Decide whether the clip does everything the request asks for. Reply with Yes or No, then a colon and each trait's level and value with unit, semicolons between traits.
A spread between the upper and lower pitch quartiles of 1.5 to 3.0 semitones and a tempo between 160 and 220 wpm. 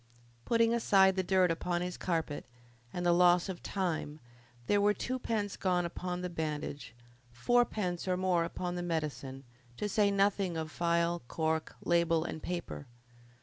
No: narrow, 2.6 semitones; average, 150 wpm